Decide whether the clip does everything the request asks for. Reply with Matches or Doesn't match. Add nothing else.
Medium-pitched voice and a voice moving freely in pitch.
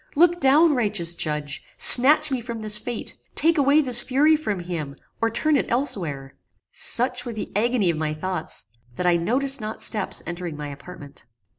Doesn't match